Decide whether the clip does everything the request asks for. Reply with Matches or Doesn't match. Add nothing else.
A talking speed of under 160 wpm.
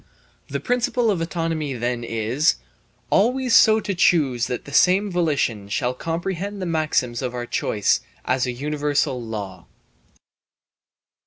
Matches